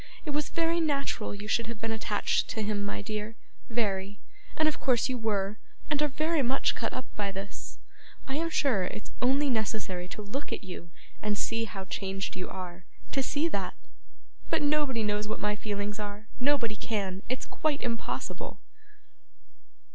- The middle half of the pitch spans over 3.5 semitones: Yes, average, 5.0 semitones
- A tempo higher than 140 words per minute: Yes, average, 175 wpm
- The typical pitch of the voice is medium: No, high, 220 Hz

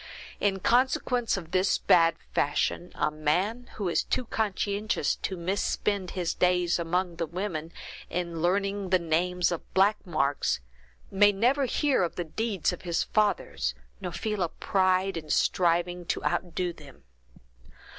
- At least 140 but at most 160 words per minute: Yes, average, 145 wpm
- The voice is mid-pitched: Yes, medium, 180 Hz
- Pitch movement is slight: No, average, 3.1 semitones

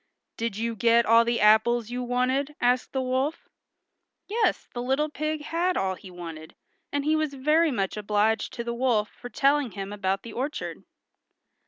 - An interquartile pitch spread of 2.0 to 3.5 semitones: No, average, 4.8 semitones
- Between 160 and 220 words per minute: Yes, average, 175 wpm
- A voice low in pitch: No, high, 245 Hz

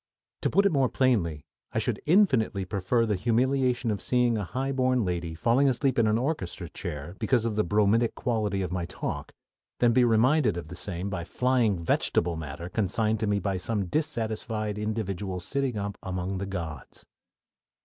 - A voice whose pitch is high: No, low, 110 Hz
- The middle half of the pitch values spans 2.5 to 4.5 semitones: No, average, 5.0 semitones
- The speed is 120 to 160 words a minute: No, average, 175 wpm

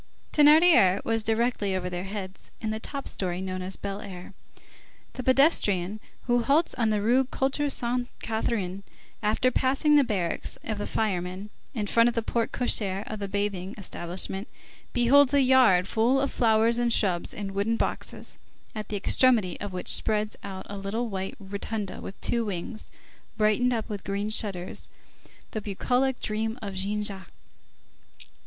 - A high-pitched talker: Yes, high, 215 Hz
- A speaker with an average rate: Yes, average, 160 wpm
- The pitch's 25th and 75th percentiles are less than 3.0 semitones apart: No, average, 3.7 semitones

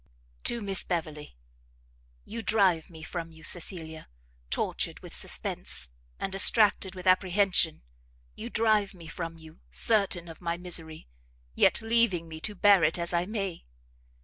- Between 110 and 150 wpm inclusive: Yes, average, 145 wpm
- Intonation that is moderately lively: Yes, average, 3.7 semitones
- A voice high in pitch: No, medium, 180 Hz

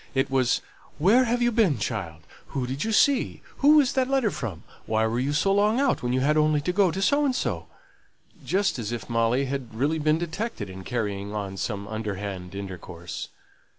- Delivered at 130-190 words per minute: No, average, 200 wpm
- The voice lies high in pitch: No, low, 135 Hz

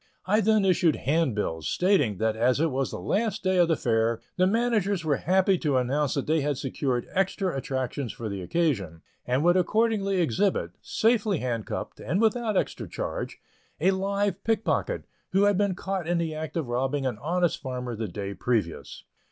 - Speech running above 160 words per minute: Yes, average, 180 wpm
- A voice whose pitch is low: No, medium, 160 Hz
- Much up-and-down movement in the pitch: Yes, wide, 7.5 semitones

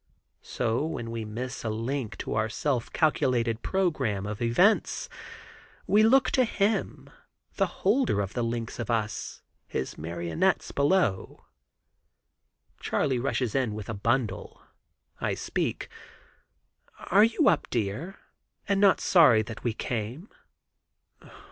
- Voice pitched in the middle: No, low, 120 Hz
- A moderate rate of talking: No, slow, 125 wpm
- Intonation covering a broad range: Yes, wide, 7.9 semitones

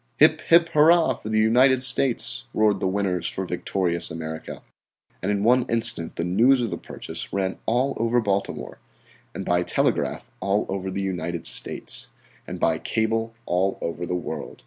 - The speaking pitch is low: Yes, low, 105 Hz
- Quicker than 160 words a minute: Yes, average, 170 wpm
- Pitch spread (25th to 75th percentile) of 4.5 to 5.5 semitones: Yes, average, 5.1 semitones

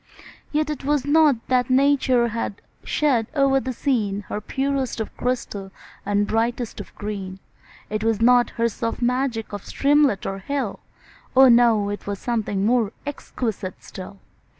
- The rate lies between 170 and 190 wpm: No, average, 150 wpm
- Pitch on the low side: No, high, 235 Hz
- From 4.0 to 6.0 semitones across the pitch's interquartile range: Yes, average, 4.4 semitones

